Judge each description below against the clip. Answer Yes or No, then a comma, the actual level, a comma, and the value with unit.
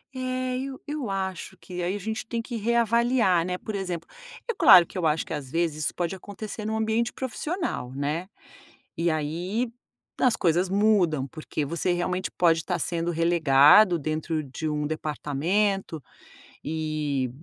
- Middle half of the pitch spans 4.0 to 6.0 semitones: Yes, wide, 5.5 semitones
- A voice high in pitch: No, medium, 175 Hz